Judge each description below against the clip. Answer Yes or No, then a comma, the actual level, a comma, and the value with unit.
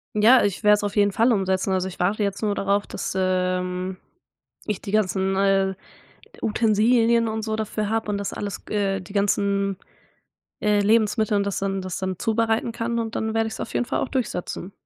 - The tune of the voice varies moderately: No, narrow, 2.3 semitones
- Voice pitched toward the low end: No, high, 205 Hz